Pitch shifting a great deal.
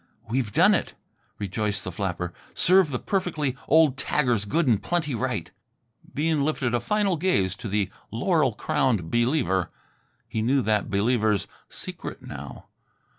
Yes: wide, 6.7 semitones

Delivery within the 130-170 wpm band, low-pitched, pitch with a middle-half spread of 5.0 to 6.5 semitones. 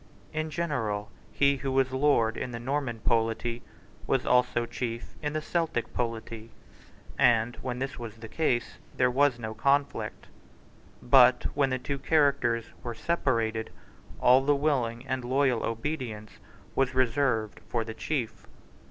No: average, 145 wpm; low, 125 Hz; average, 3.3 semitones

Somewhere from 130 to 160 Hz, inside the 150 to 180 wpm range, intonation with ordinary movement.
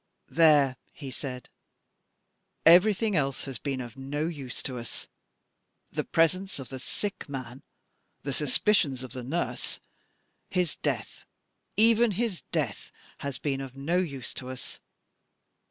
No: medium, 140 Hz; slow, 135 wpm; average, 5.0 semitones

